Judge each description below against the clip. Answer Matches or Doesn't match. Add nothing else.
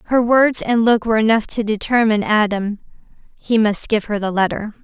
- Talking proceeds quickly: Doesn't match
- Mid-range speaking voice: Doesn't match